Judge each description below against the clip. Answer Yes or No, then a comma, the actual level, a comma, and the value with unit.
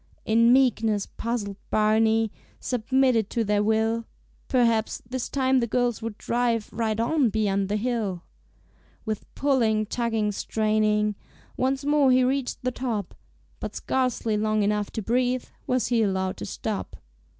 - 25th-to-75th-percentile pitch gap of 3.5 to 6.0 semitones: No, average, 2.8 semitones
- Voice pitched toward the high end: Yes, high, 225 Hz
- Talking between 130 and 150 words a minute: Yes, average, 140 wpm